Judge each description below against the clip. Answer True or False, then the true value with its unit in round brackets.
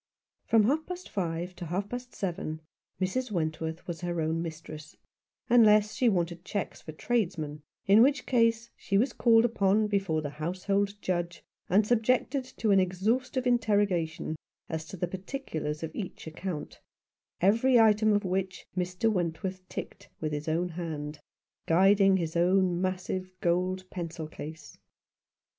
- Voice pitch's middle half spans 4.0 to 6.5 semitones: True (4.5 semitones)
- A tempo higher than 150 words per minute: False (145 wpm)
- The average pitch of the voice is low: False (185 Hz)